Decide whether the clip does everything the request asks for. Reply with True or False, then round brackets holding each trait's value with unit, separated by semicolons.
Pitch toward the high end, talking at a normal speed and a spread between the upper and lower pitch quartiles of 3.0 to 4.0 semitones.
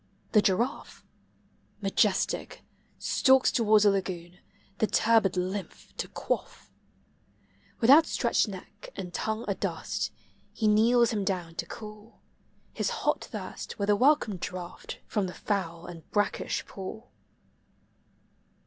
False (205 Hz; 120 wpm; 3.4 semitones)